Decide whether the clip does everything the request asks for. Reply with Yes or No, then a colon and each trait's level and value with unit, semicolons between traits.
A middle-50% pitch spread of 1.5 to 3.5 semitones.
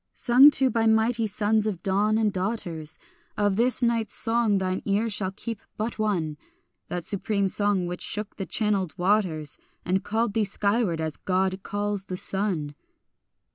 Yes: average, 2.9 semitones